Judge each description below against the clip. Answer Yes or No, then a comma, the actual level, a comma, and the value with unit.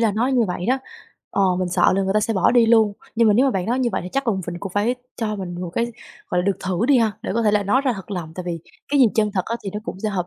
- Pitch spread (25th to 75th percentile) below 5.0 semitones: Yes, average, 3.6 semitones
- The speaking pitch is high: Yes, high, 210 Hz